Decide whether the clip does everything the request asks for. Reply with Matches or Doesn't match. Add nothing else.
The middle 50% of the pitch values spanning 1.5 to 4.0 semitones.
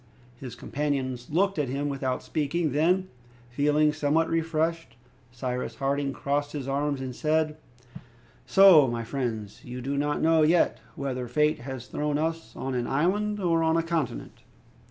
Matches